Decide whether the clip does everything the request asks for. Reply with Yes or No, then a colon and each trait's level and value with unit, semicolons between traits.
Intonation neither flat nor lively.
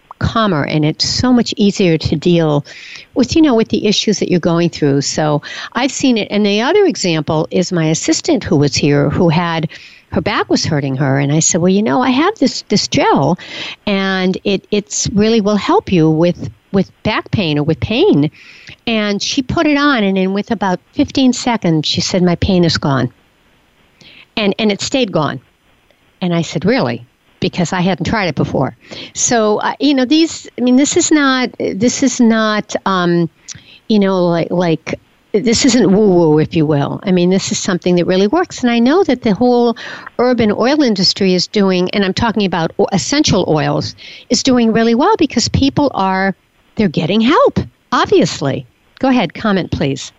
No: wide, 6.3 semitones